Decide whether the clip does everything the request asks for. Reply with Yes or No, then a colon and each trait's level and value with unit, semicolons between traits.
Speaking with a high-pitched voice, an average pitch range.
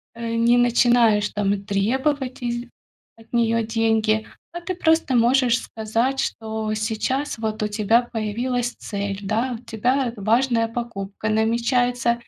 No: high, 230 Hz; narrow, 2.1 semitones